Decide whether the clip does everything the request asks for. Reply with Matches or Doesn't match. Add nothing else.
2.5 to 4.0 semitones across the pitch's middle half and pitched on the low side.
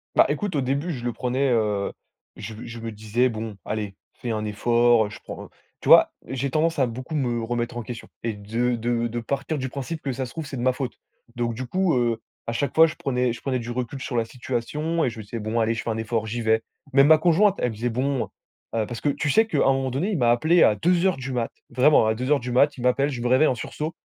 Matches